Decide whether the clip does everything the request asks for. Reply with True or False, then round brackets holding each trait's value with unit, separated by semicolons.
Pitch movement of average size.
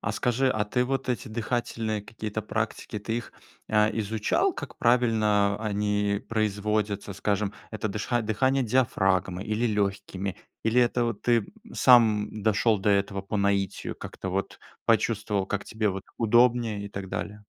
False (2.3 semitones)